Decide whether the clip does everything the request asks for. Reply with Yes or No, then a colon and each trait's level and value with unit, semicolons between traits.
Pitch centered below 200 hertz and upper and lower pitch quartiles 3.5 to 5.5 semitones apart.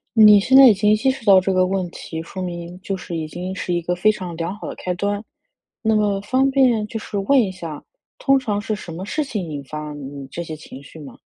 Yes: high, 190 Hz; average, 4.0 semitones